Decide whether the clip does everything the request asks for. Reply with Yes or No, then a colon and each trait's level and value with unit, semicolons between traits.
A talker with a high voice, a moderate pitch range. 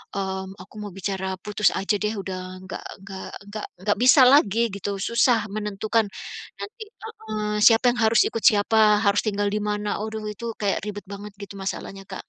No: high, 210 Hz; narrow, 2.0 semitones